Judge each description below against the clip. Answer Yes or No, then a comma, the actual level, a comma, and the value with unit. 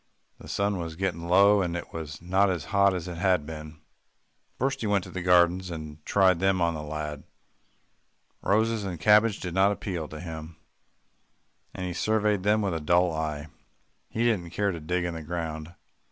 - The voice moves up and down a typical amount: Yes, average, 3.6 semitones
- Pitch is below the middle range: Yes, very low, 90 Hz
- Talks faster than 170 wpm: Yes, average, 190 wpm